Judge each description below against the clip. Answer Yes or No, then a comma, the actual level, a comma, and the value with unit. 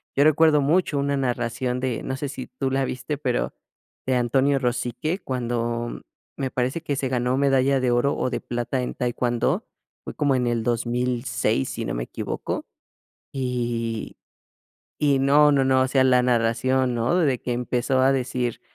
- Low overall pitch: Yes, low, 130 Hz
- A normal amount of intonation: No, narrow, 2.1 semitones